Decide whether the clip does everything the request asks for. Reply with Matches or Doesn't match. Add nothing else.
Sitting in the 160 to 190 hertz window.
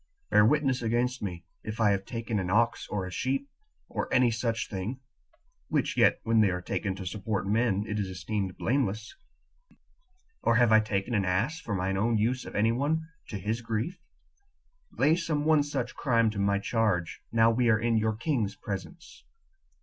Doesn't match